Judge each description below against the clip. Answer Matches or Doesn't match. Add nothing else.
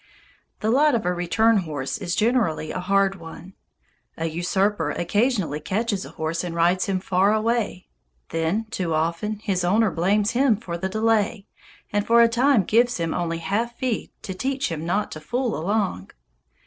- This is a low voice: Doesn't match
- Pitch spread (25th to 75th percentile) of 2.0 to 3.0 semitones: Doesn't match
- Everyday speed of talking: Matches